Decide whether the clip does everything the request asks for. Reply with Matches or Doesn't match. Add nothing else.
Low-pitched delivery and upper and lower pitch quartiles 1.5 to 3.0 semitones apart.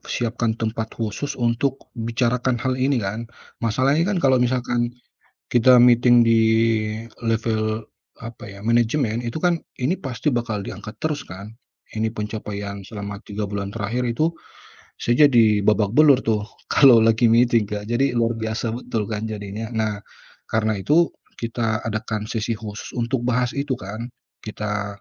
Matches